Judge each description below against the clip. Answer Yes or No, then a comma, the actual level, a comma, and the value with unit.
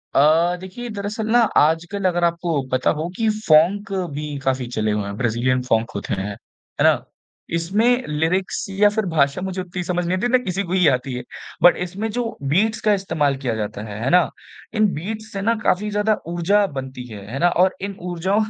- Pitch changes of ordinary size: No, wide, 6.5 semitones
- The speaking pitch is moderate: Yes, medium, 175 Hz